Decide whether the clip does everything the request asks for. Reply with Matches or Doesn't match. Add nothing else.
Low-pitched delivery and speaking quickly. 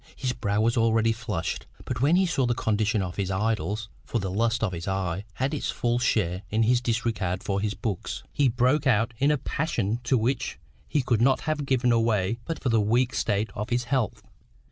Matches